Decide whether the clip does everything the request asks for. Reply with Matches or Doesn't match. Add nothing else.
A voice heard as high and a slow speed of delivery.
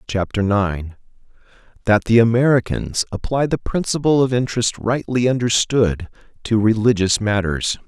Doesn't match